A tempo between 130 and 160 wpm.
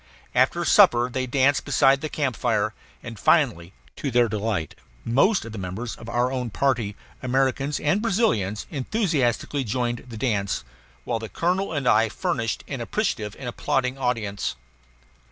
Yes: average, 155 wpm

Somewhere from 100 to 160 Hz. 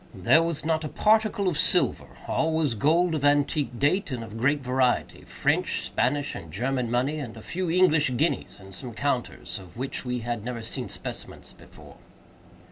Yes: medium, 140 Hz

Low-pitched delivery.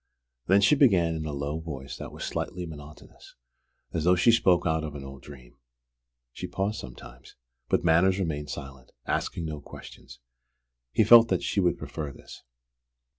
Yes: very low, 80 Hz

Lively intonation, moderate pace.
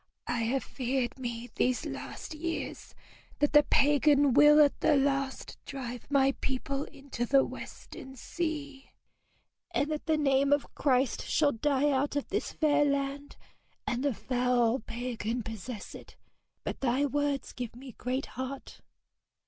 No: narrow, 2.5 semitones; average, 145 wpm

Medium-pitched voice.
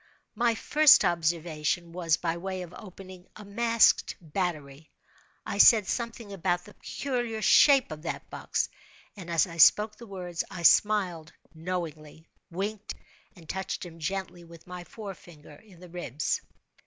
Yes: medium, 180 Hz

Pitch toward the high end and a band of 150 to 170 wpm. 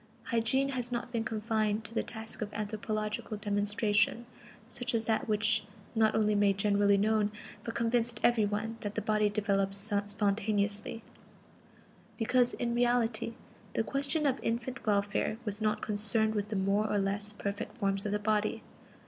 Yes: high, 215 Hz; average, 155 wpm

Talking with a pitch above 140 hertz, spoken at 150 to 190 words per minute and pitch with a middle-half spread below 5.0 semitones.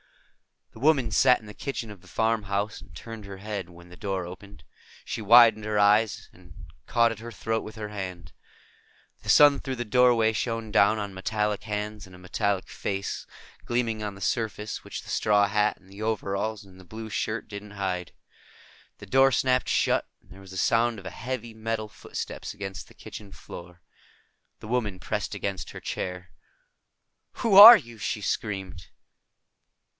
No: low, 105 Hz; average, 175 wpm; narrow, 2.6 semitones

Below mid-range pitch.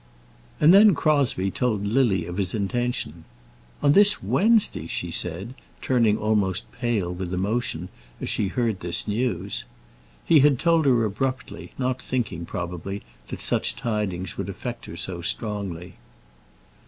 Yes: low, 105 Hz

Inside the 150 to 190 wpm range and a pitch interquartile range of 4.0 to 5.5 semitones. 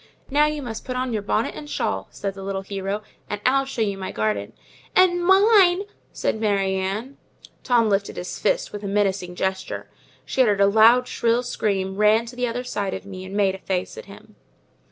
No: fast, 205 wpm; average, 4.3 semitones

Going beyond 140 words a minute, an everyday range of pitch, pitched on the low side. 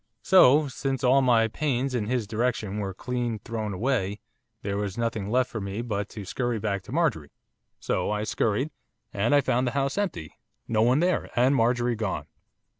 Yes: average, 185 wpm; average, 3.7 semitones; low, 120 Hz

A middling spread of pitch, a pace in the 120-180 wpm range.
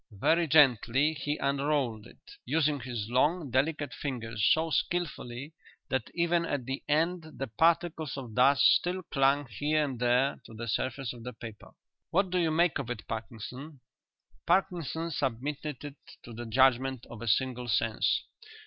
Yes: average, 4.6 semitones; average, 160 wpm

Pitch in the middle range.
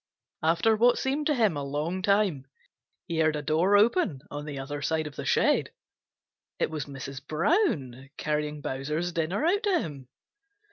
Yes: medium, 155 Hz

